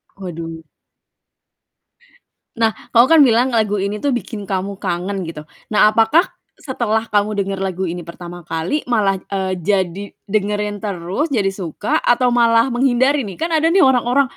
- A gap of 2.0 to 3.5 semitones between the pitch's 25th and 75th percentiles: No, average, 4.2 semitones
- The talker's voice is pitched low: No, high, 210 Hz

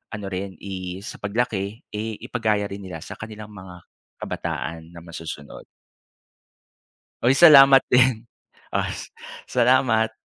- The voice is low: Yes, low, 105 Hz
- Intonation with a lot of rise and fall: No, average, 4.0 semitones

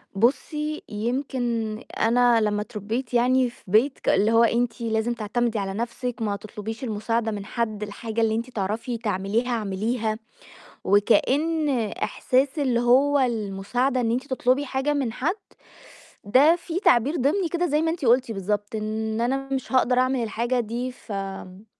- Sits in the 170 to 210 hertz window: No, high, 235 Hz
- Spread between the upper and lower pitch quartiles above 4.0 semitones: No, average, 3.1 semitones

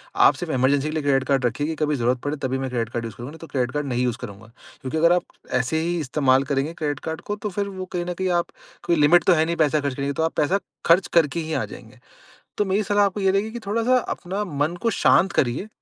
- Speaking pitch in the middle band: Yes, medium, 155 Hz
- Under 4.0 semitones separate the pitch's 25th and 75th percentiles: No, average, 4.9 semitones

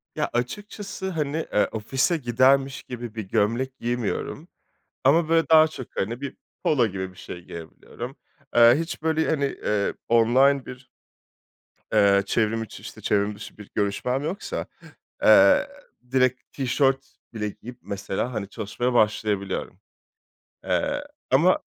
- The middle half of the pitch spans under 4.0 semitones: No, average, 4.6 semitones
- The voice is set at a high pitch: No, low, 120 Hz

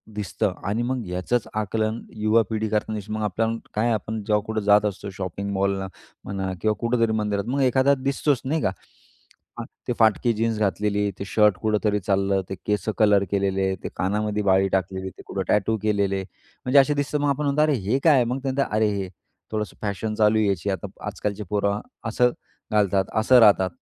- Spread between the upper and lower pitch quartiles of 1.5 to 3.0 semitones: Yes, narrow, 2.6 semitones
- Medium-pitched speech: No, low, 105 Hz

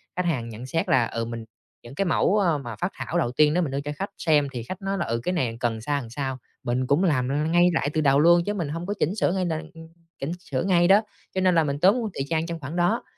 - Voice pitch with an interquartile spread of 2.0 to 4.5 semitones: No, average, 5.3 semitones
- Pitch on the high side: No, medium, 155 Hz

